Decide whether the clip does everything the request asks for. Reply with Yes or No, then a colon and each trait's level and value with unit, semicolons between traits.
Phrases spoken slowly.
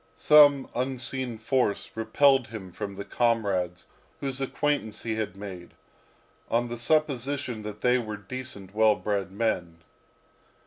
Yes: slow, 130 wpm